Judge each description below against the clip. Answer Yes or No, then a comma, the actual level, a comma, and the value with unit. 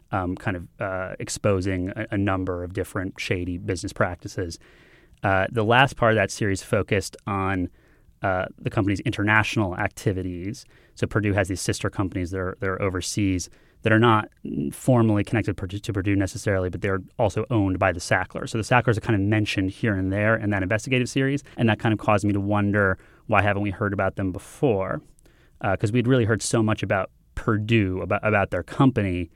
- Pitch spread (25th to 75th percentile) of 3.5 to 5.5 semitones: No, average, 2.9 semitones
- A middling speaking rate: Yes, average, 195 wpm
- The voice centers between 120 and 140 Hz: No, low, 100 Hz